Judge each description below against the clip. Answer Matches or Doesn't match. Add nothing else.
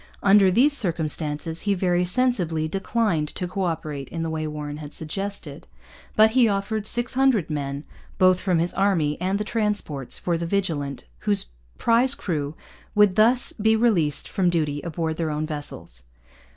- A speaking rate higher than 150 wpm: Matches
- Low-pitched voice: Doesn't match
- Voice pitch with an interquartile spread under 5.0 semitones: Doesn't match